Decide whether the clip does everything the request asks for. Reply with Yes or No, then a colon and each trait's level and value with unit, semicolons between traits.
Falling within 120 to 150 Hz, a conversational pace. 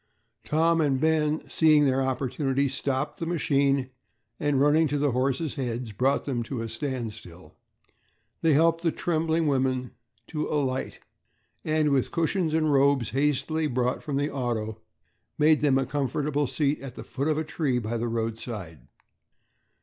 Yes: medium, 140 Hz; average, 155 wpm